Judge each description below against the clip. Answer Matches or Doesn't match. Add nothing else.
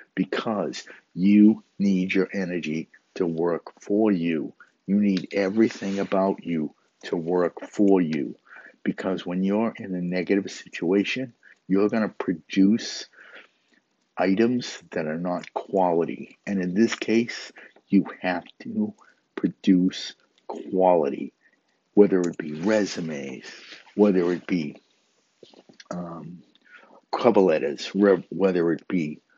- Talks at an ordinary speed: Doesn't match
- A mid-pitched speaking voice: Doesn't match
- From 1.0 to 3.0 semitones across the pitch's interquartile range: Matches